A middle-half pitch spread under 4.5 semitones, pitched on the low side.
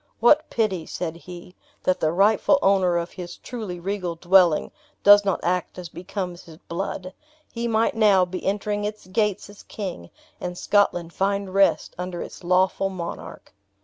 No: narrow, 2.6 semitones; medium, 185 Hz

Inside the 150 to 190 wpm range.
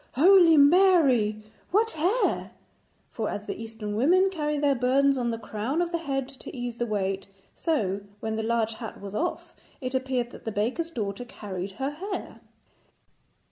Yes: average, 170 wpm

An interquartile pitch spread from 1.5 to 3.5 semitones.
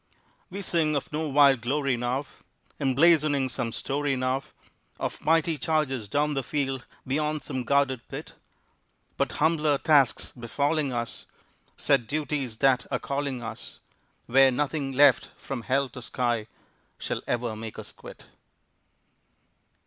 Yes: average, 2.8 semitones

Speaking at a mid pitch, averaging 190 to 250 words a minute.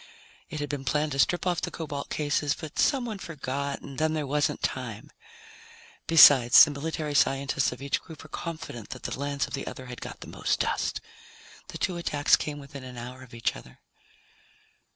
Yes: medium, 145 Hz; average, 195 wpm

